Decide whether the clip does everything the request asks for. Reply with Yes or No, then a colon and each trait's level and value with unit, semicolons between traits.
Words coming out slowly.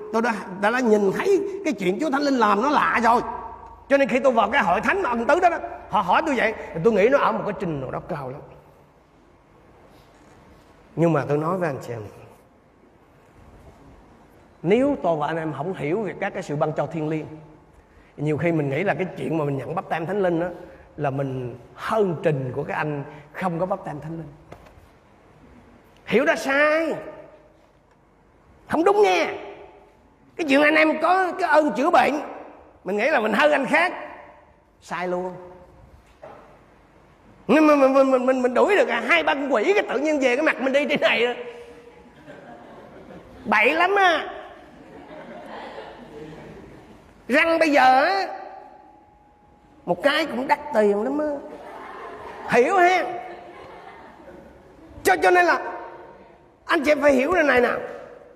No: average, 175 wpm